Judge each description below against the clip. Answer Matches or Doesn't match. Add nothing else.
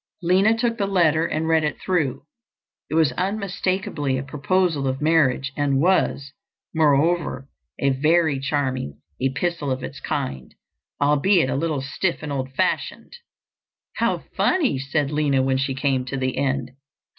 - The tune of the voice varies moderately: Matches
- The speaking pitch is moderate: Matches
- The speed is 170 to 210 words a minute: Doesn't match